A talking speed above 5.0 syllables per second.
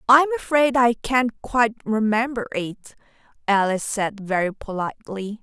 No: 4.6 syllables/s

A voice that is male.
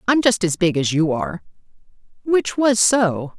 No: female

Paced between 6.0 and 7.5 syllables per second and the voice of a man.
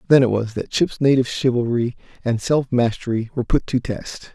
No: 5.5 syllables/s; male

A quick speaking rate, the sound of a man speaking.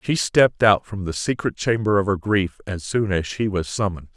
Yes: fast, 230 wpm; male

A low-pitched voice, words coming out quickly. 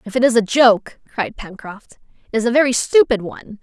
No: high, 230 Hz; fast, 215 wpm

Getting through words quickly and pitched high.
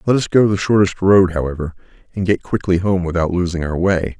No: fast, 215 wpm; very low, 95 Hz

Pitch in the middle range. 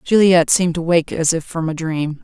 Yes: medium, 165 Hz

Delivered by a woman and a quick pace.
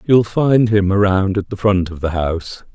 No: male; fast, 220 wpm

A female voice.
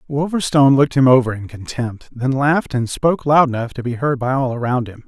No: male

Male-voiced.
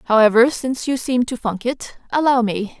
No: female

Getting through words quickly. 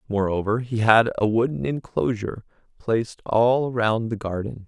No: average, 140 wpm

